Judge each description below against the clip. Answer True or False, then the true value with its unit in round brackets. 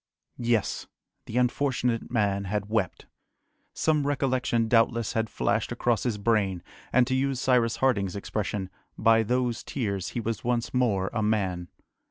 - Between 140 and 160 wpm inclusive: True (145 wpm)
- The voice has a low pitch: True (115 Hz)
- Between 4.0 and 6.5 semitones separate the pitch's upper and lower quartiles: False (3.4 semitones)